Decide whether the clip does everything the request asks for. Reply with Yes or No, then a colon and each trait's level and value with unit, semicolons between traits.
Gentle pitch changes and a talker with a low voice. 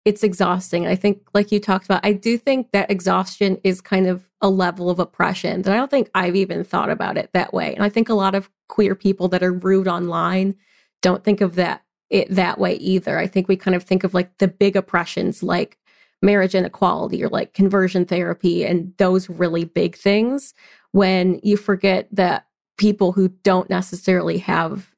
No: narrow, 1.6 semitones; high, 190 Hz